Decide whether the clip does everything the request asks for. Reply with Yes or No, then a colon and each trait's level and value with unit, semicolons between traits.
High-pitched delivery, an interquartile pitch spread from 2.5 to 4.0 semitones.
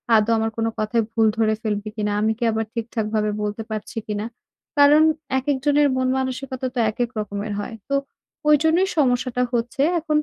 Yes: high, 235 Hz; average, 3.6 semitones